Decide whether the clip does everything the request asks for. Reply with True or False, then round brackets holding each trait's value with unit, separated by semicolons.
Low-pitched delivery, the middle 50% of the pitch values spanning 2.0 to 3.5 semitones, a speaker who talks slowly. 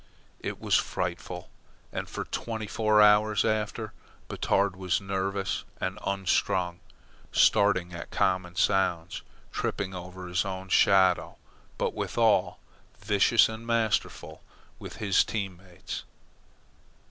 True (95 Hz; 2.6 semitones; 110 wpm)